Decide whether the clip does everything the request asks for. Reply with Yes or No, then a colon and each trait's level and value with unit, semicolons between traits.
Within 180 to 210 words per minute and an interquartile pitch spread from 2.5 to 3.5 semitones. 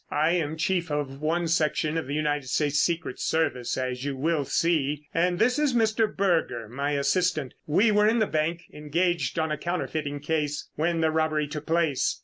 Yes: average, 185 wpm; average, 2.8 semitones